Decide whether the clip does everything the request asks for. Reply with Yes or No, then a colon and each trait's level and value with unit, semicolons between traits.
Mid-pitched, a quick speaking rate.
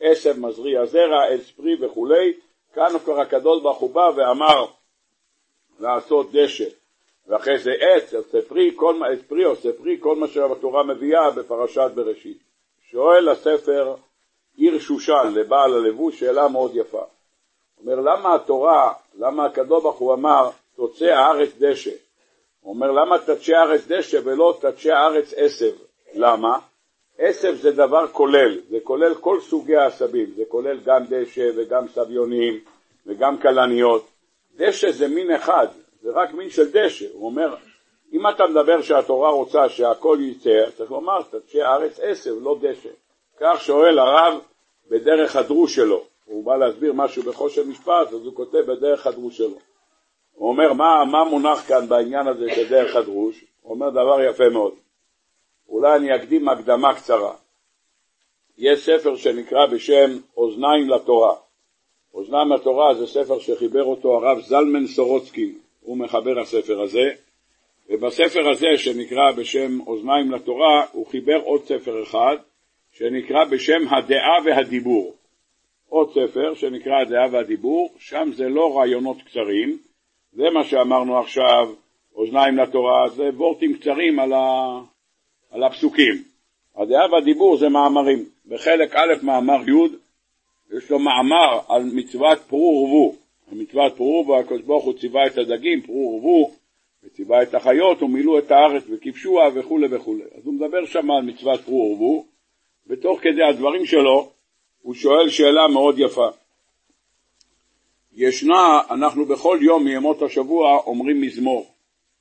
No: medium, 175 Hz; average, 140 wpm